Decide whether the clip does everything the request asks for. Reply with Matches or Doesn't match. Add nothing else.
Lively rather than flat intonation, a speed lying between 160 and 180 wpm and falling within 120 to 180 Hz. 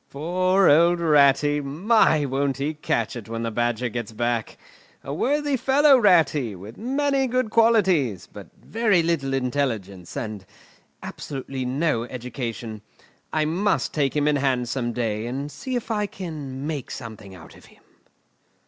Doesn't match